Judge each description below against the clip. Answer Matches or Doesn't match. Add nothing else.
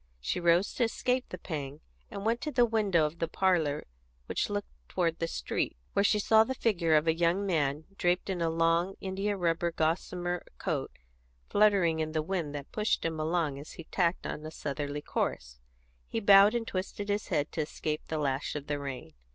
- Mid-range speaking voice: Matches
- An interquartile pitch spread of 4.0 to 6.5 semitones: Matches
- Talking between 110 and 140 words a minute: Doesn't match